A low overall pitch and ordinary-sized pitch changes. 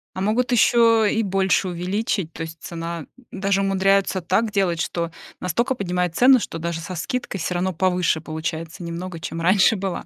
No: medium, 185 Hz; average, 3.0 semitones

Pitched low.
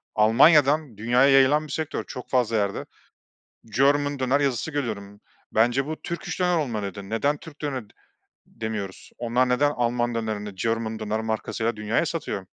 Yes: low, 120 Hz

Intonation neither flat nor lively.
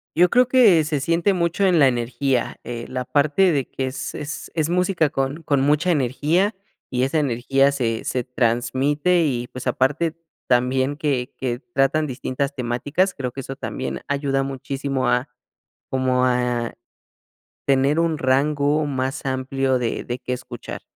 Yes: average, 3.1 semitones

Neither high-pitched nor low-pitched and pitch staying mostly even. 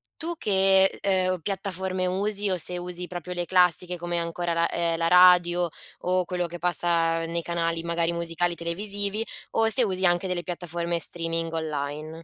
Yes: medium, 175 Hz; narrow, 1.7 semitones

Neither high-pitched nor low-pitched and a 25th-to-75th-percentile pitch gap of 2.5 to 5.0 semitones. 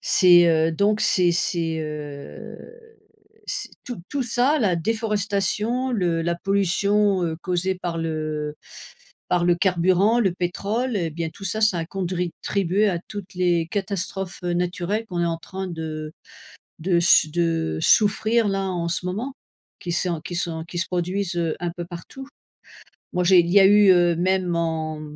Yes: medium, 180 Hz; average, 2.9 semitones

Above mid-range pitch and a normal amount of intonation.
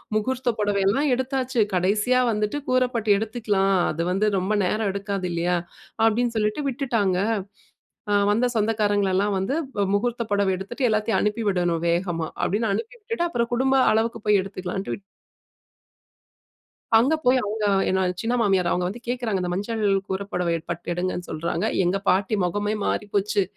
Yes: high, 210 Hz; average, 3.6 semitones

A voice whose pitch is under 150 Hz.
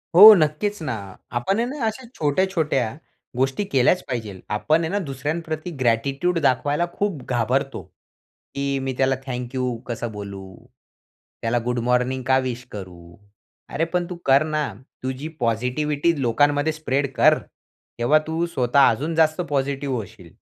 Yes: low, 135 Hz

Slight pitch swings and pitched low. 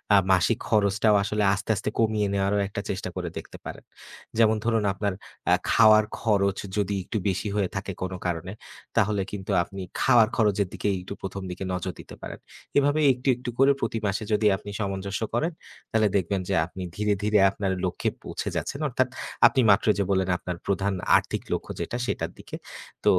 Yes: narrow, 2.2 semitones; low, 100 Hz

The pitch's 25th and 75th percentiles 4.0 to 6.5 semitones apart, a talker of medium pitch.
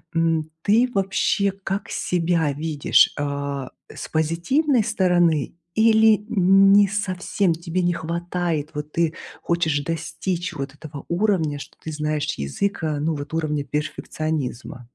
Yes: average, 4.3 semitones; medium, 165 Hz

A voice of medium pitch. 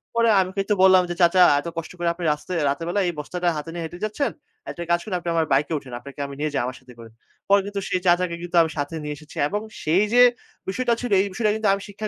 Yes: medium, 175 Hz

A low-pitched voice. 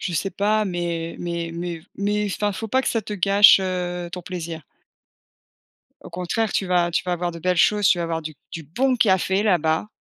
No: medium, 180 Hz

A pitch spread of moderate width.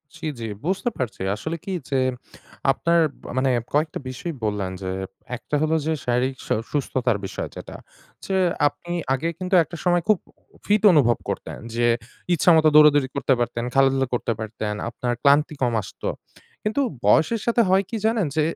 No: wide, 5.7 semitones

